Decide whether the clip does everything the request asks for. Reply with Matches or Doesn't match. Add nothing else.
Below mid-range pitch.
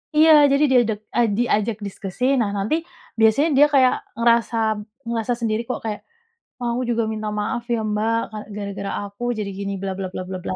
Doesn't match